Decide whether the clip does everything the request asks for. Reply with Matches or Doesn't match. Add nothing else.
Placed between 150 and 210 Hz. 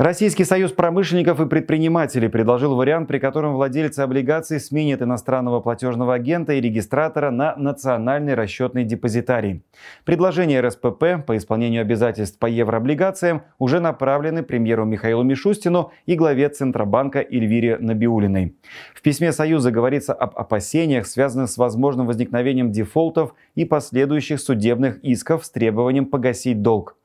Doesn't match